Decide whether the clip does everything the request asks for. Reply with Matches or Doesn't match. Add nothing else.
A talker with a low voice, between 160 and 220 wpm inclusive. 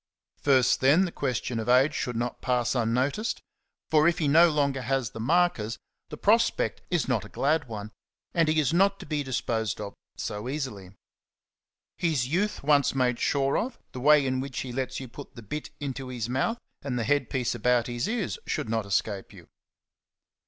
Matches